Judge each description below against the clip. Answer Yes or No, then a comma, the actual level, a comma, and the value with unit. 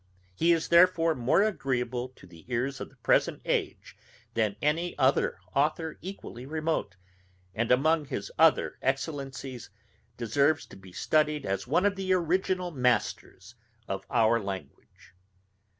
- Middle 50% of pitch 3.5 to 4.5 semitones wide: No, wide, 5.6 semitones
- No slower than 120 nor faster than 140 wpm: Yes, slow, 135 wpm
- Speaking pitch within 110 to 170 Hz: Yes, medium, 140 Hz